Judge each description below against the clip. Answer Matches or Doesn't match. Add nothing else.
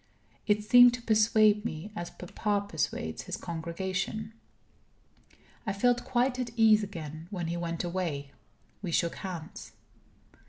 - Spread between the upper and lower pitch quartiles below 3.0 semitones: Doesn't match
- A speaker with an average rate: Doesn't match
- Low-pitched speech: Doesn't match